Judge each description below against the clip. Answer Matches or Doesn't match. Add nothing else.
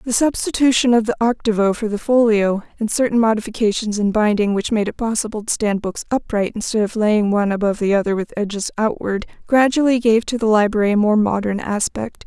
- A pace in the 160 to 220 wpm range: Matches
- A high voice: Matches